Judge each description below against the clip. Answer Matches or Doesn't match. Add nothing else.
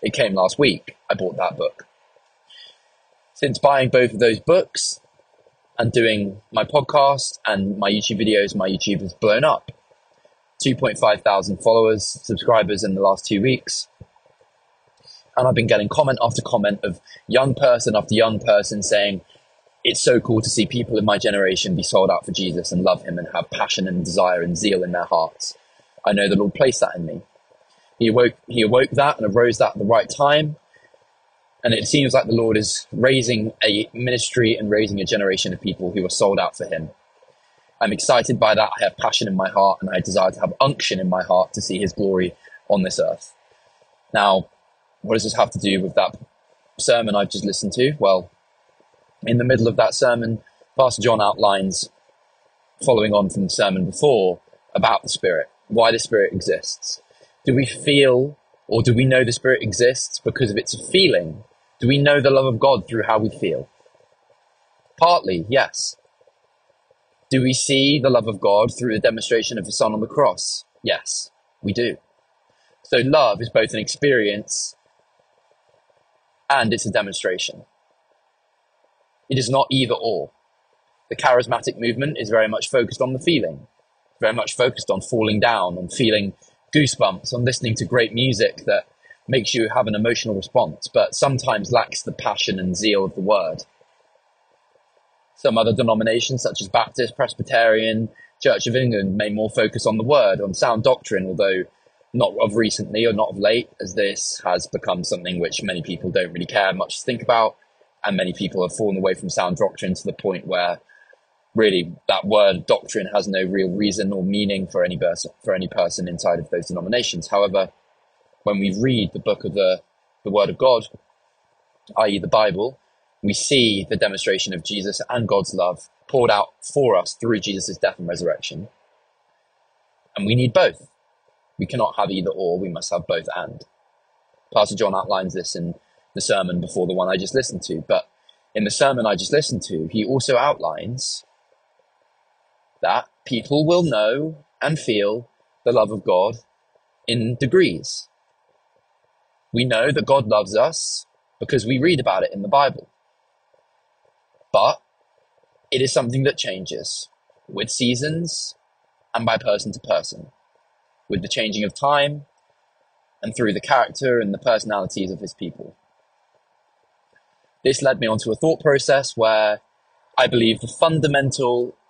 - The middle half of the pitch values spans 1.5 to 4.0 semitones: Doesn't match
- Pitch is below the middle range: Matches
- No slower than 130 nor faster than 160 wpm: Doesn't match